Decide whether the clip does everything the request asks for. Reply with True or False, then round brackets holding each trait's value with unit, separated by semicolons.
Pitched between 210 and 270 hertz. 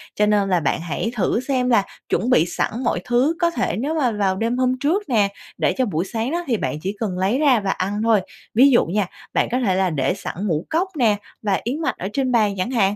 True (220 Hz)